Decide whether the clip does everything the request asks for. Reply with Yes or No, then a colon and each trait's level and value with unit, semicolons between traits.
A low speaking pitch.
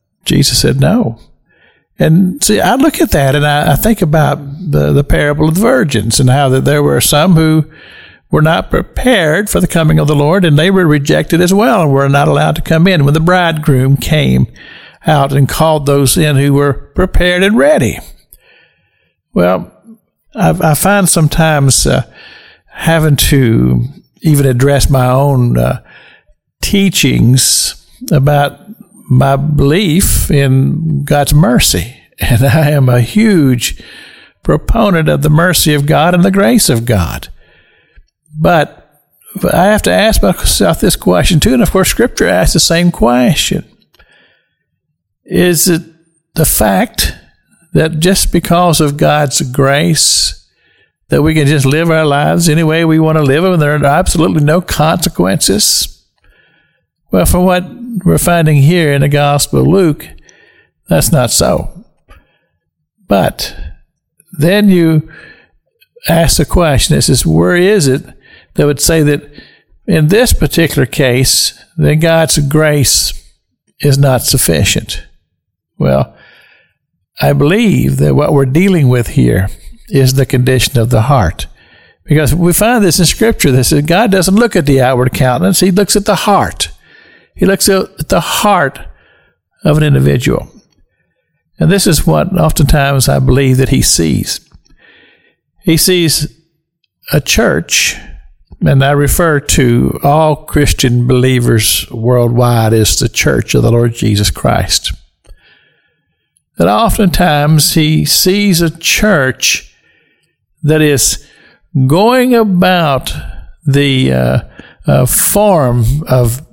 No: medium, 150 Hz